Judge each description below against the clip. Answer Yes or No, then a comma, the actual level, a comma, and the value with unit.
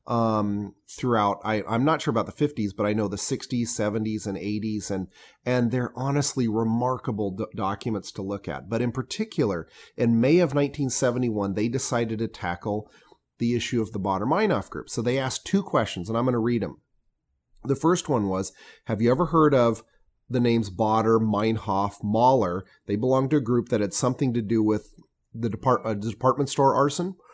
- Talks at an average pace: Yes, average, 190 wpm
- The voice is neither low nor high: No, low, 115 Hz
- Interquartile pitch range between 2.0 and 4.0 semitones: Yes, average, 3.6 semitones